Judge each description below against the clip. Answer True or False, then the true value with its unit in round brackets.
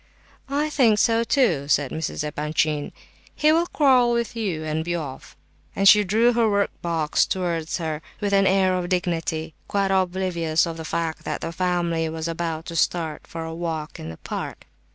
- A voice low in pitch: False (170 Hz)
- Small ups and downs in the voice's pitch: False (4.1 semitones)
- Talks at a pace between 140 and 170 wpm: False (180 wpm)